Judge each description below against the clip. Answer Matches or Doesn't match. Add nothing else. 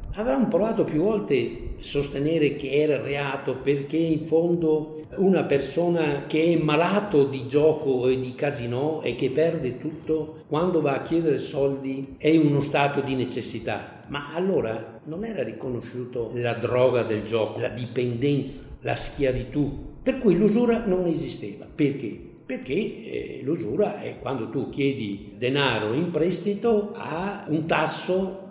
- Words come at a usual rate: Matches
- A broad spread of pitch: Doesn't match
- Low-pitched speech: Doesn't match